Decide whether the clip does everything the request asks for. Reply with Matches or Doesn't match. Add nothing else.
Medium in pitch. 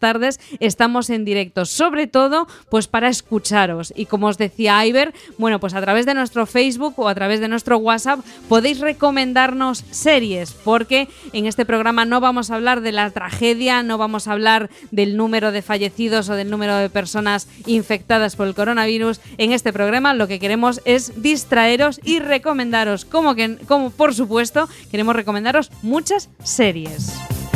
Doesn't match